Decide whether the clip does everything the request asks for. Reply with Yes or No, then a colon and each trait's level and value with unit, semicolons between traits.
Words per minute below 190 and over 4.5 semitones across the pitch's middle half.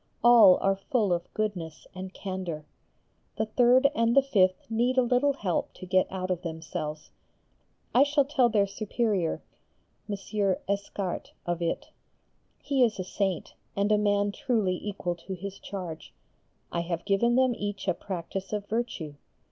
No: average, 155 wpm; average, 4.1 semitones